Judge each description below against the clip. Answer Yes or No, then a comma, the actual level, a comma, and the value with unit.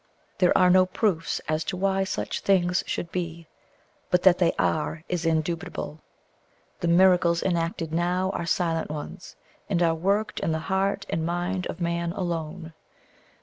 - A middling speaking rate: Yes, average, 155 wpm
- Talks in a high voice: No, medium, 175 Hz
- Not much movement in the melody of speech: Yes, narrow, 1.9 semitones